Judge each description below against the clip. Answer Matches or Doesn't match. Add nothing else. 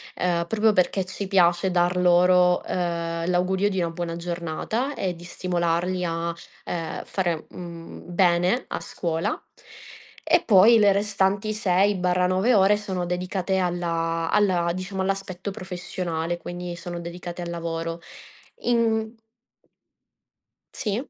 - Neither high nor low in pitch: Matches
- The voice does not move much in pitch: Matches